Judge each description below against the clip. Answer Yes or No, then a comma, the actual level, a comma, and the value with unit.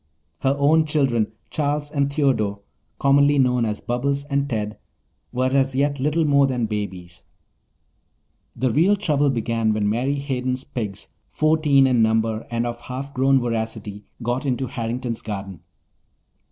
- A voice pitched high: No, low, 130 Hz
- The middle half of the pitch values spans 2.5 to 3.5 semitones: No, average, 3.9 semitones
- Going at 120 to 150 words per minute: Yes, average, 140 wpm